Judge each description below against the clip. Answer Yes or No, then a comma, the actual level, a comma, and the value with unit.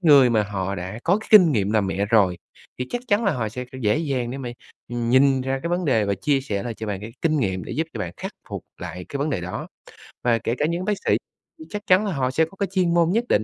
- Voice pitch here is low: Yes, low, 130 Hz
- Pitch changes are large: Yes, wide, 8.0 semitones